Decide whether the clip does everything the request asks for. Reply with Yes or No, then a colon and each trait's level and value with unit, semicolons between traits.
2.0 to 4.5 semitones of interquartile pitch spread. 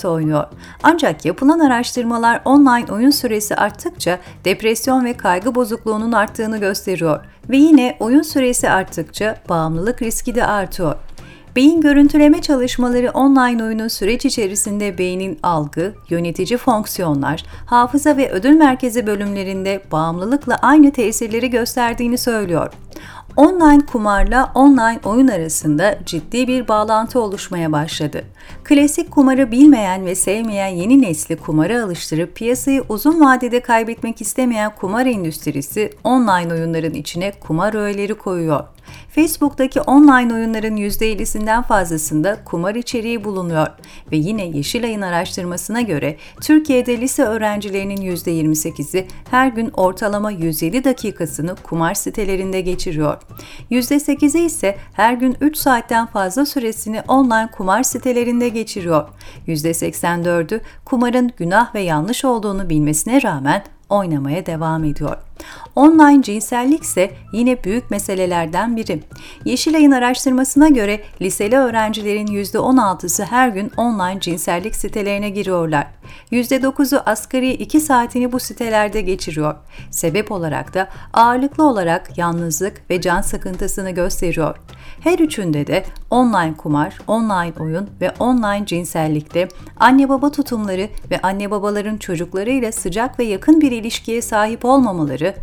No: wide, 5.6 semitones